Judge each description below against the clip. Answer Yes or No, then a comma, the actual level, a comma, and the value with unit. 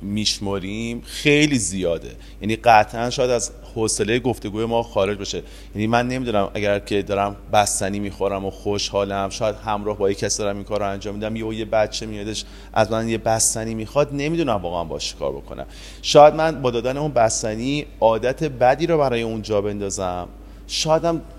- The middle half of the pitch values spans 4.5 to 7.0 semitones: No, average, 2.9 semitones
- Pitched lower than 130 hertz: Yes, low, 110 Hz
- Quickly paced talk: Yes, fast, 170 wpm